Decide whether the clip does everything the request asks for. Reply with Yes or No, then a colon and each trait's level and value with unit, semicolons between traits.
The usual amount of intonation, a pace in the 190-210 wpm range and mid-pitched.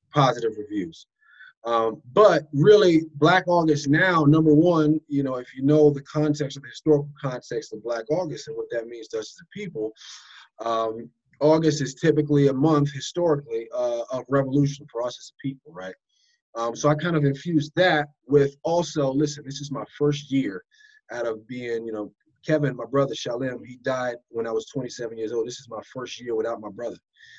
Yes: average, 4.7 semitones; average, 195 wpm; medium, 145 Hz